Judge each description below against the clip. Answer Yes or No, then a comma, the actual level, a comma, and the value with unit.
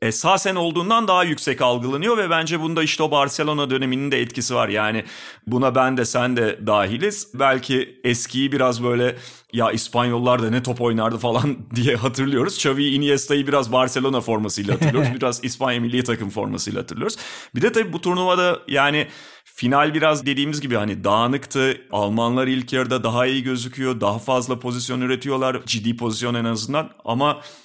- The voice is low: Yes, low, 130 Hz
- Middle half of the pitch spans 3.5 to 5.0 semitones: No, average, 3.0 semitones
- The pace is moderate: No, fast, 160 wpm